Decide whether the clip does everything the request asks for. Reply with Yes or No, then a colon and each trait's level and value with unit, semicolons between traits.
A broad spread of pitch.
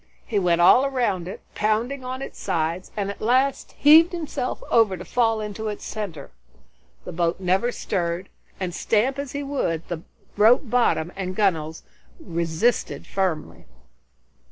Yes: wide, 5.9 semitones